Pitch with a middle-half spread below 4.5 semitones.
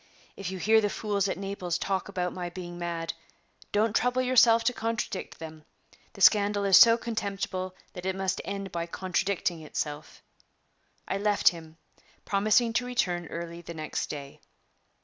Yes: average, 3.3 semitones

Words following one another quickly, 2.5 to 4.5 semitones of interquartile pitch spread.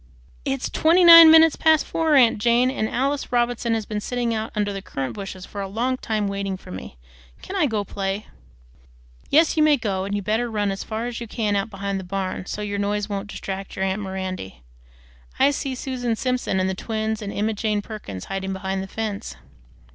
Yes: fast, 215 wpm; average, 3.8 semitones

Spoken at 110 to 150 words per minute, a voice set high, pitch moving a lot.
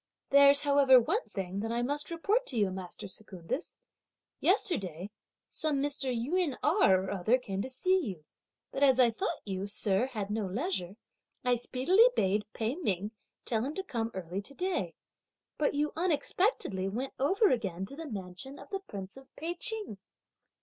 No: average, 170 wpm; very high, 250 Hz; wide, 7.3 semitones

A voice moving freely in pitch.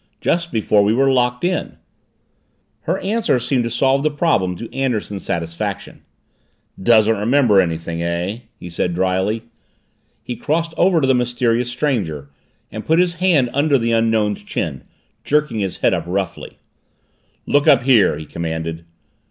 Yes: wide, 6.7 semitones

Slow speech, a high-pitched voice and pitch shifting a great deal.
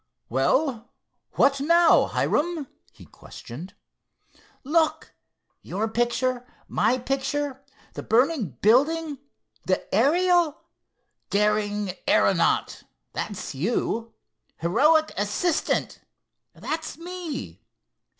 Yes: slow, 70 wpm; very high, 260 Hz; wide, 6.9 semitones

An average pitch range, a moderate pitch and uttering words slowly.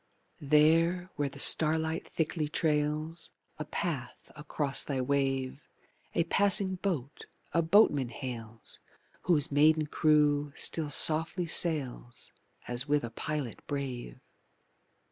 Yes: average, 3.0 semitones; medium, 150 Hz; slow, 110 wpm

